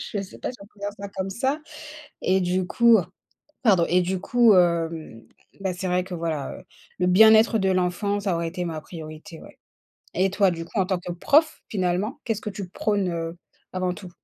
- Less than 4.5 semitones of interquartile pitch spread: Yes, average, 2.7 semitones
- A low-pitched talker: No, medium, 185 Hz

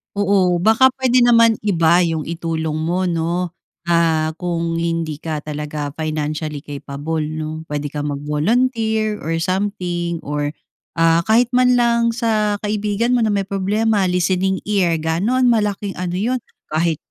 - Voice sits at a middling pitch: Yes, medium, 175 Hz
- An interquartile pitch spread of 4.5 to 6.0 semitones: Yes, average, 4.9 semitones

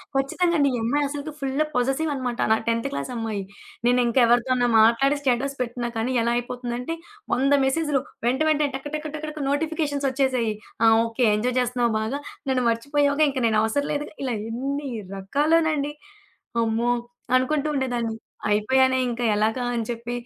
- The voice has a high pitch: Yes, very high, 260 Hz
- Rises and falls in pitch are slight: No, average, 3.2 semitones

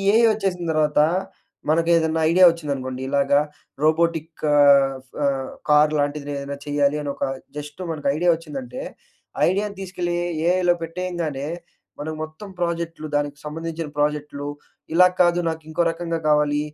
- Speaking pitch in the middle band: Yes, medium, 155 Hz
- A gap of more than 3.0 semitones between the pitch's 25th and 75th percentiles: No, average, 2.7 semitones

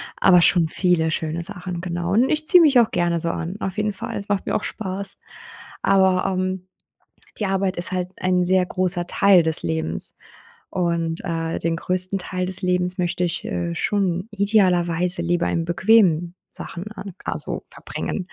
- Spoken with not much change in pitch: Yes, narrow, 2.2 semitones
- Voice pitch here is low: No, medium, 180 Hz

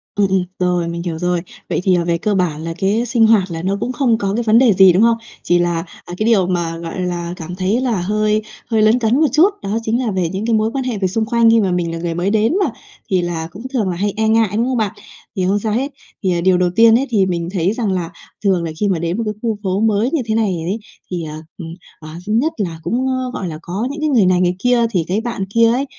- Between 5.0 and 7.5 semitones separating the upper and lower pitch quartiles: No, average, 4.3 semitones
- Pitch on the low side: No, high, 200 Hz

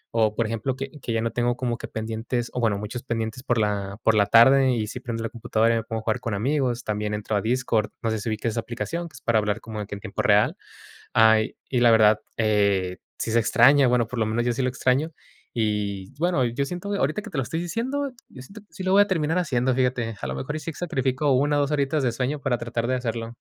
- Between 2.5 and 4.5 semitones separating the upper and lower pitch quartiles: Yes, average, 3.5 semitones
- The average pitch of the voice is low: Yes, low, 120 Hz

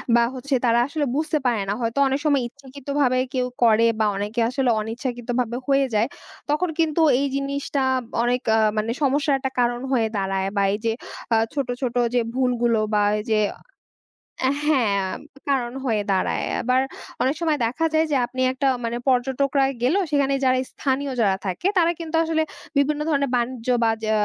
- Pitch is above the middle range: Yes, very high, 255 Hz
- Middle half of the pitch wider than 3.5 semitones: No, average, 3.2 semitones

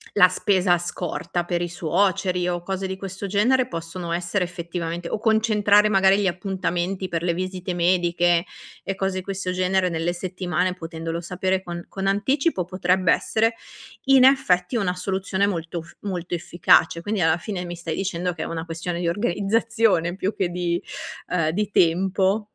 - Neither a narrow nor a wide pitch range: No, narrow, 2.2 semitones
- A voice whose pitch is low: No, medium, 180 Hz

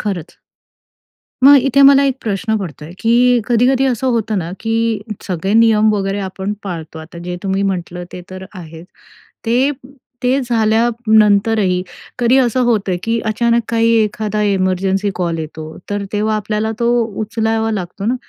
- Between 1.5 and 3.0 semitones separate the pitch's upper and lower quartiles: No, average, 3.5 semitones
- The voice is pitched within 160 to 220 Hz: Yes, high, 215 Hz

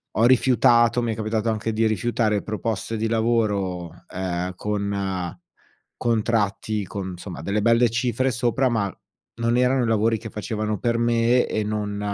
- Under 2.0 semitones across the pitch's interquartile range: No, narrow, 2.4 semitones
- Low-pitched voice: Yes, low, 110 Hz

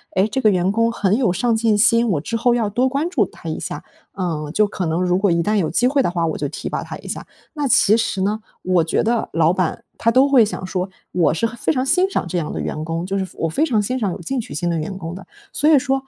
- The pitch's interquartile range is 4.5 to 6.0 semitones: Yes, average, 5.3 semitones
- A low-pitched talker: No, high, 205 Hz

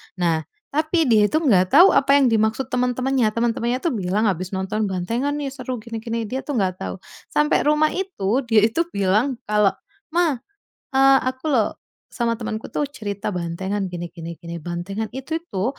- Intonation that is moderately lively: No, wide, 5.7 semitones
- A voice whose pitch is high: Yes, high, 225 Hz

